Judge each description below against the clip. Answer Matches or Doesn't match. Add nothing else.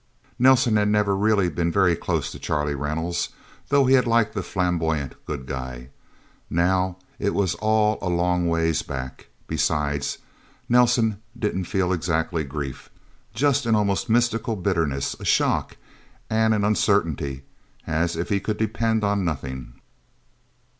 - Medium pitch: Doesn't match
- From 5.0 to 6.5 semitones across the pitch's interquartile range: Matches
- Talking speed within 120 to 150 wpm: Matches